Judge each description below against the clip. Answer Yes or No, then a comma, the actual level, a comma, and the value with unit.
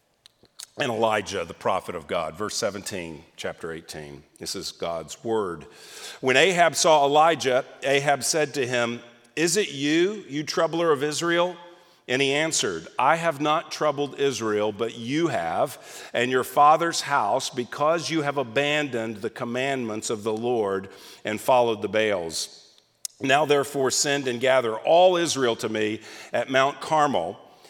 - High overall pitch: No, medium, 140 Hz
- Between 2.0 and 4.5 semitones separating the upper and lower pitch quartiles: No, average, 4.9 semitones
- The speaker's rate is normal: Yes, average, 150 wpm